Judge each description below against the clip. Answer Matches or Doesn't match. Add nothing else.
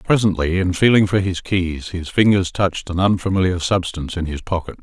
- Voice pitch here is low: Matches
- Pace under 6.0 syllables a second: Matches